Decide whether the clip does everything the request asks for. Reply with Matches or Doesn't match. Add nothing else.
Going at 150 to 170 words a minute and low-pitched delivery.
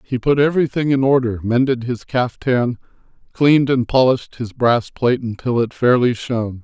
Matches